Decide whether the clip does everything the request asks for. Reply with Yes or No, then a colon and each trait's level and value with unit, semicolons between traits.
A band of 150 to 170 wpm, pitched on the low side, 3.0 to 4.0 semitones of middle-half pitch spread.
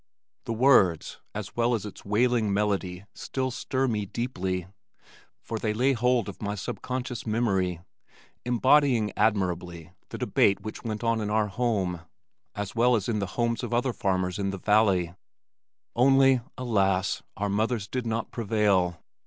Yes: average, 155 wpm; low, 110 Hz; average, 3.7 semitones